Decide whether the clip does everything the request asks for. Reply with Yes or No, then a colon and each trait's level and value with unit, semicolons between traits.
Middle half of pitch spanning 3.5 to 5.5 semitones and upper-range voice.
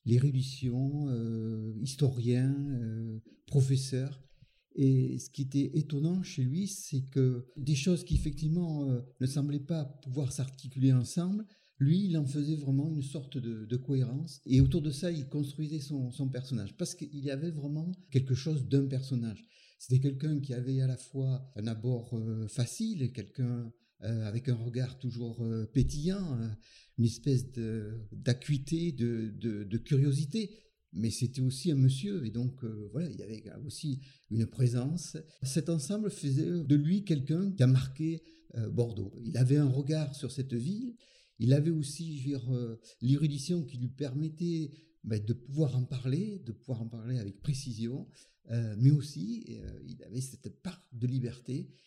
No: average, 3.9 semitones; low, 135 Hz